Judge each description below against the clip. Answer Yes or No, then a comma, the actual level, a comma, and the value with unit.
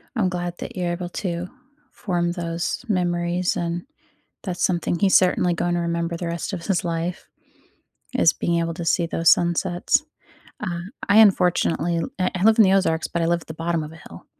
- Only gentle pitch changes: Yes, narrow, 1.4 semitones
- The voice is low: No, medium, 175 Hz